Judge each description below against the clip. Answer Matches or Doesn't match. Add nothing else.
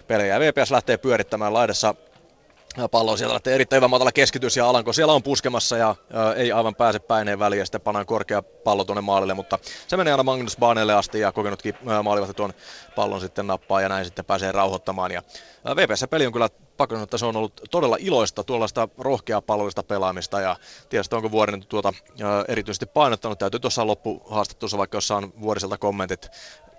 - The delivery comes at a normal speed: Doesn't match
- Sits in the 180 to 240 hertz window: Doesn't match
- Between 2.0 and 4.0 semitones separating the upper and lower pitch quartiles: Matches